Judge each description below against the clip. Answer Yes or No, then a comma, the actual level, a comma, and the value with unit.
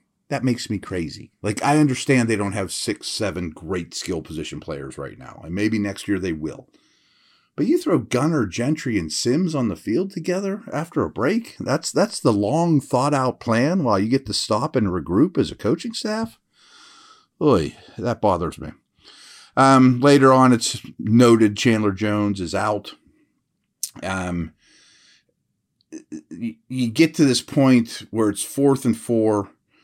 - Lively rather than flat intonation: Yes, wide, 6.5 semitones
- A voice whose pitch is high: No, low, 120 Hz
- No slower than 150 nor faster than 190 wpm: Yes, average, 160 wpm